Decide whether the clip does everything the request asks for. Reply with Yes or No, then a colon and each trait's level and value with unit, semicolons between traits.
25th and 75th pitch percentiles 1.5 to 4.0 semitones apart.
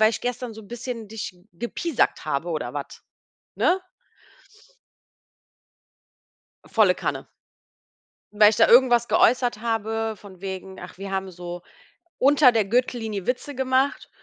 No: average, 4.4 semitones